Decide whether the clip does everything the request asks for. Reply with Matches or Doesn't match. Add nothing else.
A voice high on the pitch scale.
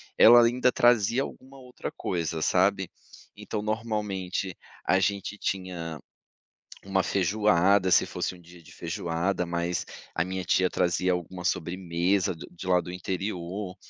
Doesn't match